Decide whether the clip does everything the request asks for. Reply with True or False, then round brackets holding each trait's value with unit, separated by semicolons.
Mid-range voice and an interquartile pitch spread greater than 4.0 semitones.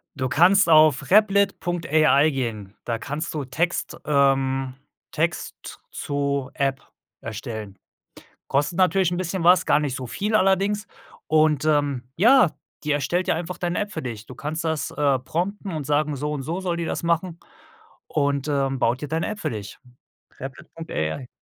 True (150 Hz; 4.4 semitones)